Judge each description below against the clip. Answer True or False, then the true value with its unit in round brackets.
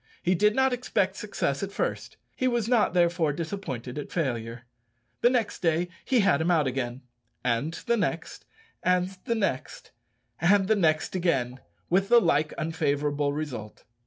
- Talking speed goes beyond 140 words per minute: True (155 wpm)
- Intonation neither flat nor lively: False (6.1 semitones)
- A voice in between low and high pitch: True (170 Hz)